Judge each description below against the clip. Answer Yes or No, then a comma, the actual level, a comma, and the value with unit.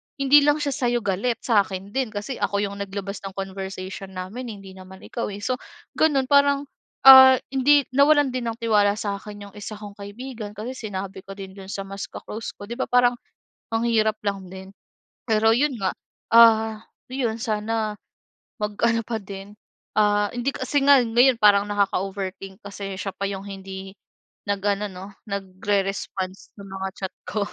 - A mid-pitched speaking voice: No, high, 205 Hz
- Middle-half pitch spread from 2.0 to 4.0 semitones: Yes, average, 3.5 semitones